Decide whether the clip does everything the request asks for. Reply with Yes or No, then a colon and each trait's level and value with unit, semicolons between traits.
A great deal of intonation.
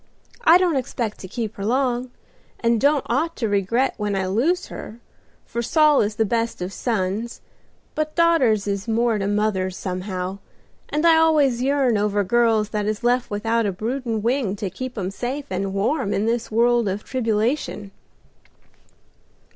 No: average, 4.0 semitones